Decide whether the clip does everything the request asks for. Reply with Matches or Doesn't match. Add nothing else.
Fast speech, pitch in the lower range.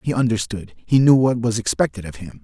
Matches